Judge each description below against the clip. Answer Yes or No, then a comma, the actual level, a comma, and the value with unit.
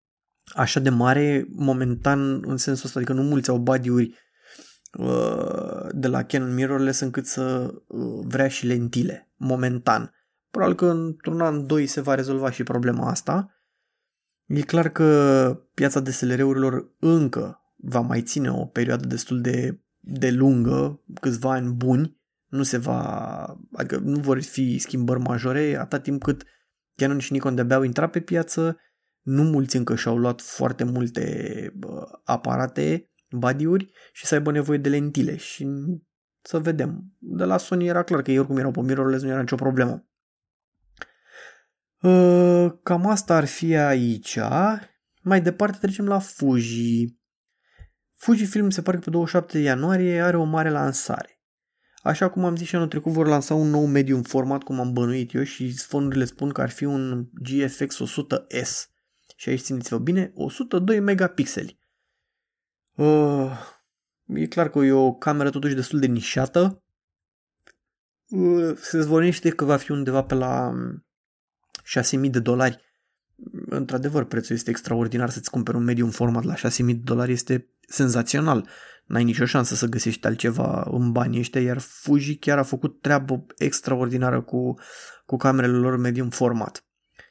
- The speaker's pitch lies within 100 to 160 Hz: Yes, low, 135 Hz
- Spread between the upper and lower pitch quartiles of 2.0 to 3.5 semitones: No, average, 4.1 semitones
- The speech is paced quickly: No, average, 150 wpm